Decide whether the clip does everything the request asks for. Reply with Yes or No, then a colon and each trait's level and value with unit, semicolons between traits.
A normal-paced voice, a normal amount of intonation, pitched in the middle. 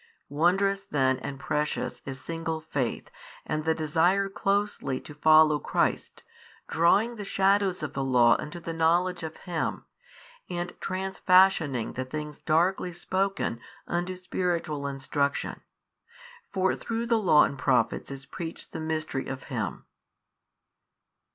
No: slow, 130 wpm; average, 4.2 semitones; medium, 160 Hz